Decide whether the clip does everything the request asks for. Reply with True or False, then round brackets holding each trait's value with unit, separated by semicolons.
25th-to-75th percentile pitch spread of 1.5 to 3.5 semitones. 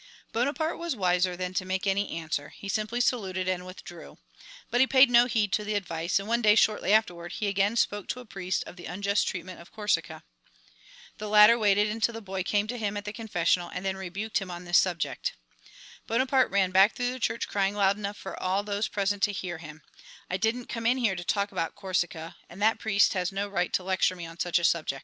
True (3.0 semitones)